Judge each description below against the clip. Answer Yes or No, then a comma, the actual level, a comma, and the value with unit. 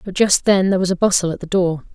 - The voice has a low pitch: No, medium, 185 Hz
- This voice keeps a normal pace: No, fast, 310 wpm